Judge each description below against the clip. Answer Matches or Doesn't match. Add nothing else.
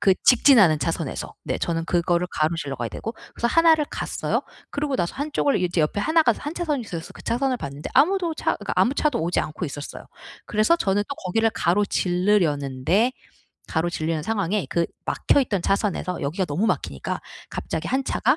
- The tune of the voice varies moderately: Doesn't match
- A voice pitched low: Doesn't match